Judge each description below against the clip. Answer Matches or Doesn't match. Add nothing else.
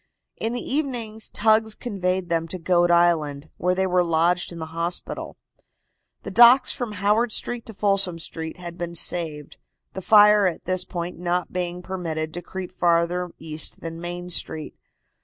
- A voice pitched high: Doesn't match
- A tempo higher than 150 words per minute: Matches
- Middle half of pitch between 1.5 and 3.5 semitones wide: Matches